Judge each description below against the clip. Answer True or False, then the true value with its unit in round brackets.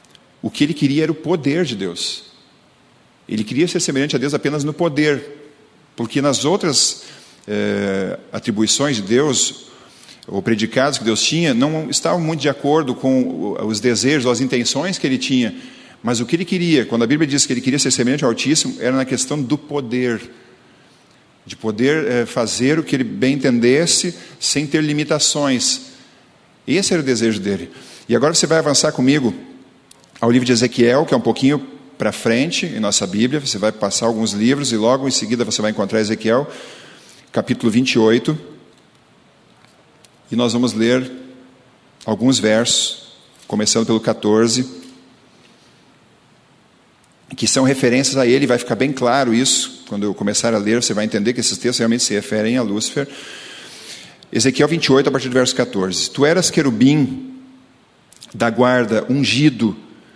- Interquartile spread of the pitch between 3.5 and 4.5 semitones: True (4.2 semitones)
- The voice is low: True (130 Hz)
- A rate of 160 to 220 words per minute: True (165 wpm)